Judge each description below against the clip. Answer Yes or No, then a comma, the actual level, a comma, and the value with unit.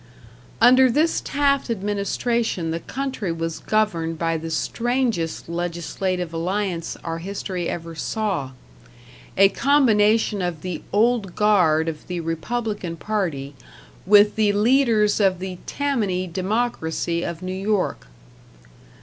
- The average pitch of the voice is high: Yes, high, 195 Hz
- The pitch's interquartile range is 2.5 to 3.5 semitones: No, average, 4.7 semitones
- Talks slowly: Yes, slow, 115 wpm